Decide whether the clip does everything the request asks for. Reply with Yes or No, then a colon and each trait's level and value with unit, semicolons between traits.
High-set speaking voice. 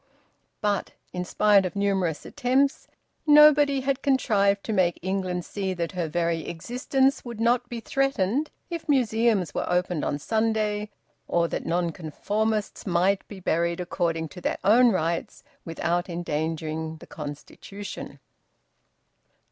Yes: high, 195 Hz